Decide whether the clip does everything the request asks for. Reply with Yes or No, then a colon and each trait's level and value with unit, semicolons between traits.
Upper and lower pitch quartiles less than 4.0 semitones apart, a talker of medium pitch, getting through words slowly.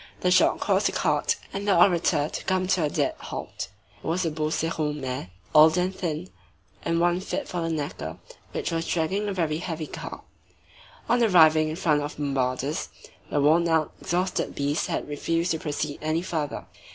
No: average, 2.8 semitones; medium, 160 Hz; average, 185 wpm